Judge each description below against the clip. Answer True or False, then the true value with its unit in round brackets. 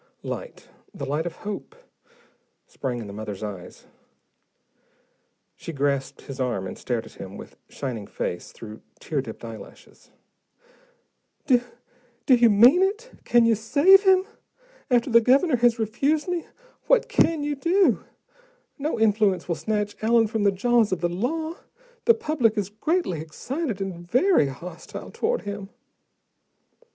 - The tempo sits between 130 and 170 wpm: True (145 wpm)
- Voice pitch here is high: True (220 Hz)